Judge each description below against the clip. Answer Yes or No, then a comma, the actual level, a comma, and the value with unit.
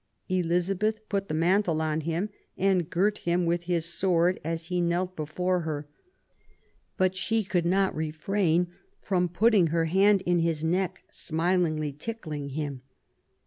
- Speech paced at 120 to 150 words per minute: Yes, average, 145 wpm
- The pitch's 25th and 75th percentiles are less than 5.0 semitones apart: Yes, average, 2.7 semitones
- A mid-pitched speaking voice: Yes, medium, 175 Hz